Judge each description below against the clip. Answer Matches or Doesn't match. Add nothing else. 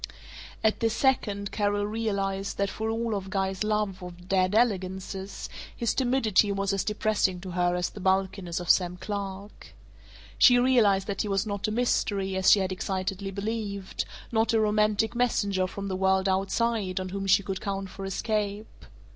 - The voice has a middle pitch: Doesn't match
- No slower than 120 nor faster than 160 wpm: Doesn't match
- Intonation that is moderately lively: Doesn't match